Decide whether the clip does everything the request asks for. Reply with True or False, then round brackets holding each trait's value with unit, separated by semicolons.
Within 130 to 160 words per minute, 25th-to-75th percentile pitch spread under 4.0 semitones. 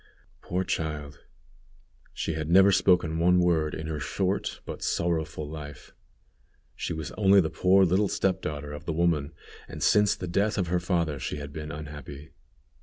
False (170 wpm; 3.3 semitones)